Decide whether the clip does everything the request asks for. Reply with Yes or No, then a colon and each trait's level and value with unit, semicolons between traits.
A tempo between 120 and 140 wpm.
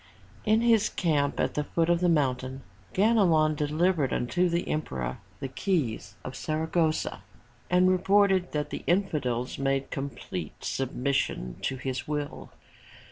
Yes: slow, 135 wpm